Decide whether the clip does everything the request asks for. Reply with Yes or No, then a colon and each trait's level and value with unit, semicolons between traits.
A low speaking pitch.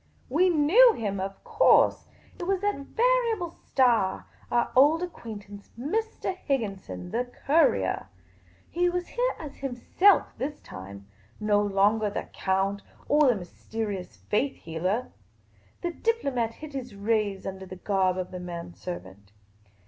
No: high, 230 Hz